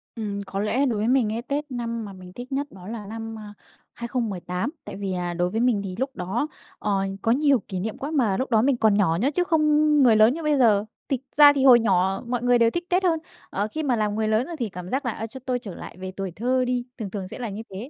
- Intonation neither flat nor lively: Yes, average, 4.4 semitones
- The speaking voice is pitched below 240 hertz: Yes, high, 225 Hz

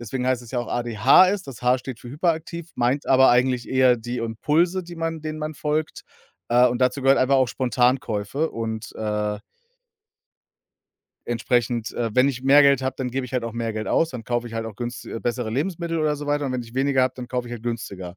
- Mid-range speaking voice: No, low, 125 Hz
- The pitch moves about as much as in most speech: Yes, average, 3.1 semitones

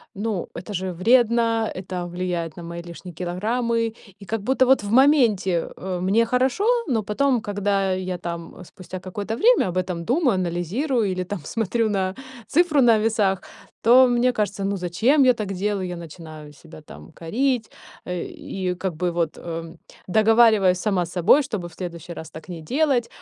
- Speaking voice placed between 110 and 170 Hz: No, high, 195 Hz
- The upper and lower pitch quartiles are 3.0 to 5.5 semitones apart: Yes, average, 4.7 semitones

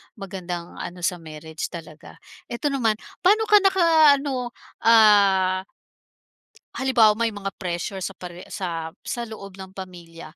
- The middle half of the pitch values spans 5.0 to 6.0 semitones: Yes, average, 5.3 semitones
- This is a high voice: Yes, high, 195 Hz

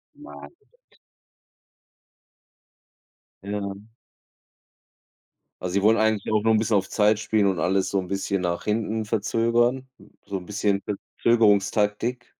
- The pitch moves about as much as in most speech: No, narrow, 2.2 semitones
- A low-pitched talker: Yes, low, 105 Hz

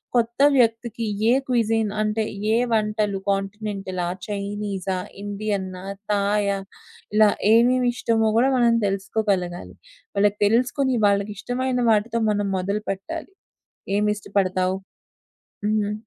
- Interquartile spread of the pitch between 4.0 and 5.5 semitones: No, narrow, 2.4 semitones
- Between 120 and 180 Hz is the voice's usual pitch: No, high, 210 Hz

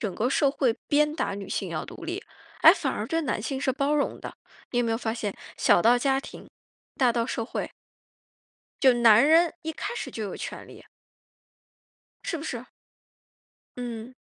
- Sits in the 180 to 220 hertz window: No, very high, 250 Hz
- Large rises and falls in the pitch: No, average, 4.4 semitones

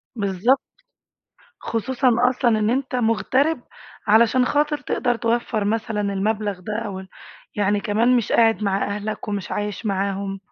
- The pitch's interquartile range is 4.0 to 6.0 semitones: No, average, 3.0 semitones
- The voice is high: Yes, high, 215 Hz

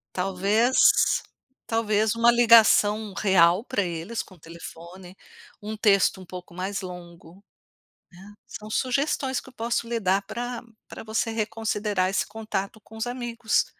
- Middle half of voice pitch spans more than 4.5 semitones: No, average, 3.6 semitones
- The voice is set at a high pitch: Yes, high, 210 Hz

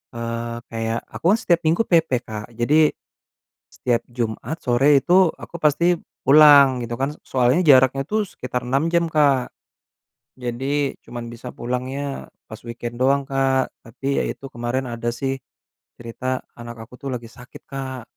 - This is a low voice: Yes, low, 130 Hz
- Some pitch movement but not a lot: Yes, average, 3.2 semitones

